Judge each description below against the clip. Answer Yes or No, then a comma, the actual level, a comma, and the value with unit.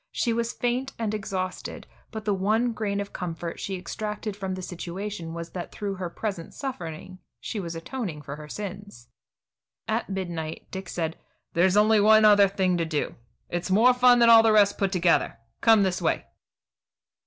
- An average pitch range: Yes, average, 3.6 semitones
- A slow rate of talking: No, average, 175 wpm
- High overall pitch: Yes, high, 195 Hz